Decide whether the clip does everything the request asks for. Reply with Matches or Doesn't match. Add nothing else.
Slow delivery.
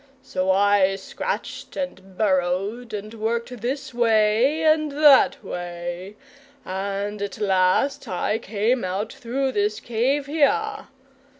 Matches